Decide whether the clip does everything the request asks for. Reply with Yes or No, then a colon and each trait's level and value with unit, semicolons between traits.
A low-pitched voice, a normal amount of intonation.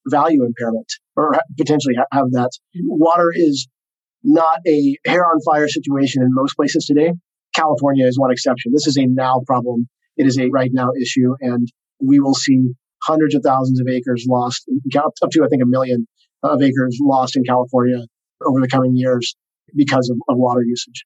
Yes: low, 130 Hz; average, 3.5 semitones